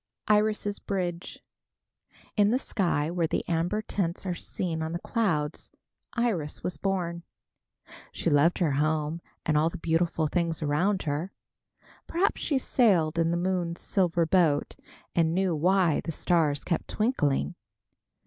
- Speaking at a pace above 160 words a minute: No, average, 140 wpm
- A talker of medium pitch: Yes, medium, 170 Hz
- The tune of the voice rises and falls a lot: No, average, 3.3 semitones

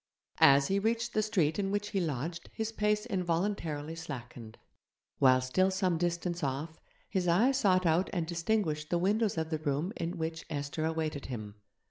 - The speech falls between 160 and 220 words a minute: Yes, average, 170 wpm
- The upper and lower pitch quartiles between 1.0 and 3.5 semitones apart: No, average, 4.3 semitones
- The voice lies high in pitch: No, medium, 170 Hz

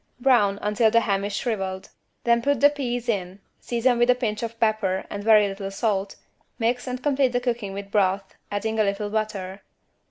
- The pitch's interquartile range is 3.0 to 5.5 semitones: Yes, average, 3.4 semitones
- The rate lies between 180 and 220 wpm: Yes, average, 190 wpm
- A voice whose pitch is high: Yes, high, 215 Hz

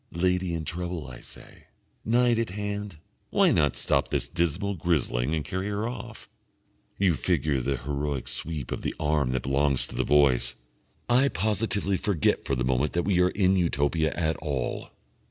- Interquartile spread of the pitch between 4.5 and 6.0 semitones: Yes, average, 5.2 semitones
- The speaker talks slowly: No, average, 170 wpm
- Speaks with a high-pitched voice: No, very low, 80 Hz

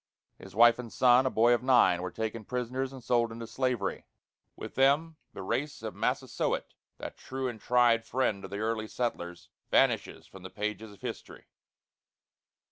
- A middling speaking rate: Yes, average, 170 wpm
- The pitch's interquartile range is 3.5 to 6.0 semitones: No, average, 3.0 semitones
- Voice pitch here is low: Yes, low, 115 Hz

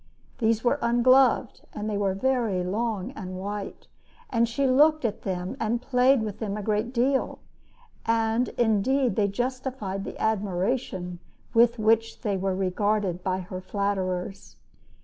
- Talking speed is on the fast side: No, average, 140 wpm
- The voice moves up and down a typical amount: Yes, average, 3.8 semitones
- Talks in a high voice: Yes, high, 215 Hz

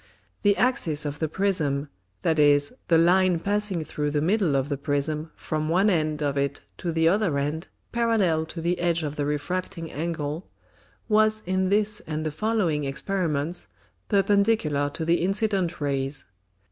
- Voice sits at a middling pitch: Yes, medium, 165 Hz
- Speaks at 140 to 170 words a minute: Yes, average, 160 wpm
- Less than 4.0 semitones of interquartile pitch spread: No, average, 4.6 semitones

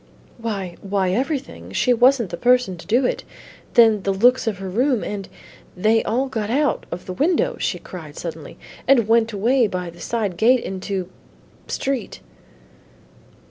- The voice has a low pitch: No, high, 225 Hz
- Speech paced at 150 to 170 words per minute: Yes, average, 160 wpm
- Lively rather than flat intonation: No, average, 4.5 semitones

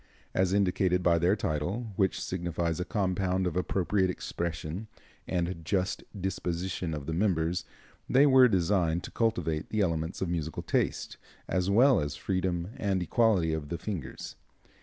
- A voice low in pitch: Yes, very low, 90 Hz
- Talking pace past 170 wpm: No, average, 150 wpm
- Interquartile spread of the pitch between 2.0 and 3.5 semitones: Yes, average, 2.7 semitones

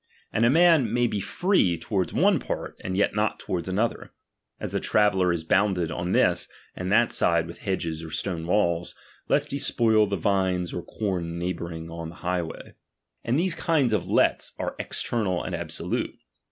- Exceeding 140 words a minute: Yes, average, 180 wpm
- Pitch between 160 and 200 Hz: No, very low, 95 Hz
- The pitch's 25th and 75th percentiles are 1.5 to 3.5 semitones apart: No, average, 4.2 semitones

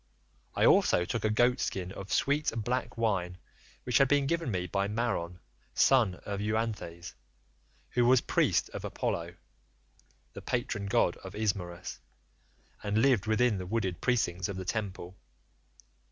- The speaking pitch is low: Yes, low, 105 Hz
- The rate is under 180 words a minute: Yes, average, 140 wpm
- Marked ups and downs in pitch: No, average, 4.5 semitones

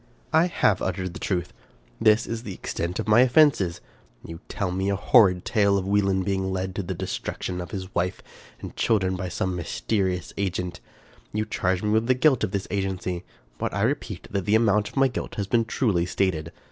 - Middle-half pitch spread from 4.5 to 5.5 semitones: No, average, 2.8 semitones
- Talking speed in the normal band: No, fast, 210 wpm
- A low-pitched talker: Yes, very low, 95 Hz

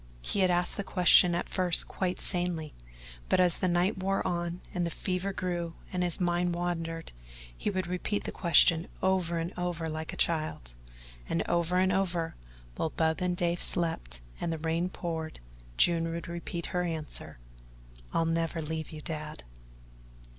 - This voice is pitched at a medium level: Yes, medium, 175 Hz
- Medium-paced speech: Yes, average, 170 wpm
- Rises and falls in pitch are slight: Yes, narrow, 1.6 semitones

